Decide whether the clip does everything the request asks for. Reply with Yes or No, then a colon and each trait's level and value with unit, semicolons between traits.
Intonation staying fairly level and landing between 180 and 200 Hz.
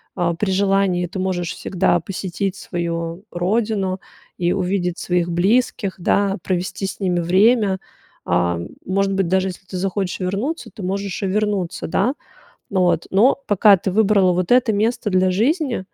Yes: narrow, 2.1 semitones; high, 190 Hz